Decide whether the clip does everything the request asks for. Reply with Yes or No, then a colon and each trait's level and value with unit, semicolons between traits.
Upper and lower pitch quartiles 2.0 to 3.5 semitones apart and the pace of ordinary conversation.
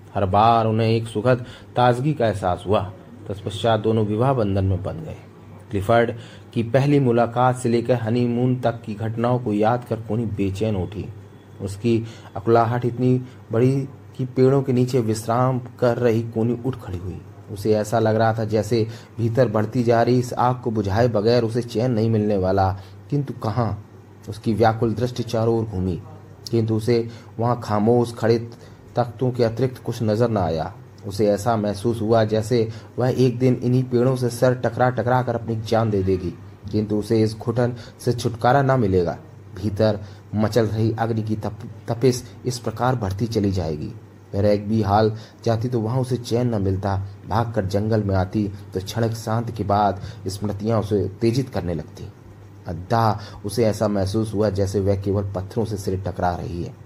Yes: average, 2.7 semitones; average, 175 wpm